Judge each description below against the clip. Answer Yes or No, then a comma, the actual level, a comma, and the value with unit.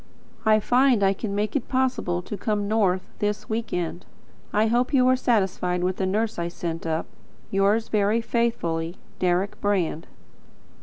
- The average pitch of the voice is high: Yes, high, 205 Hz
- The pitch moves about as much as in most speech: Yes, average, 4.0 semitones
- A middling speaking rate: Yes, average, 160 wpm